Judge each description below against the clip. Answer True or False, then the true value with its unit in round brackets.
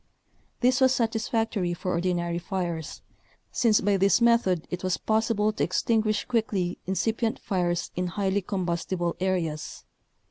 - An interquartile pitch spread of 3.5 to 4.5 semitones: True (4.0 semitones)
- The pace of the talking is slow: True (130 wpm)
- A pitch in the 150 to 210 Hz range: True (190 Hz)